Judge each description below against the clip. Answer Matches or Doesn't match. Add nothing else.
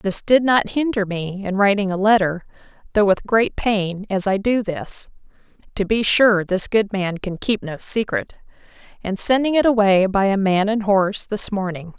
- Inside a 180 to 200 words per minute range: Matches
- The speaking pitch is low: Doesn't match